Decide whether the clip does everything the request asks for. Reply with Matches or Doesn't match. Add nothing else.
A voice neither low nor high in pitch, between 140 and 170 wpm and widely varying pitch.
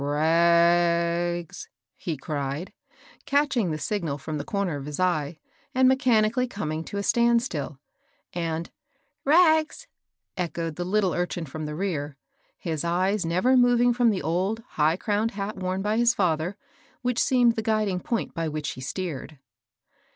Matches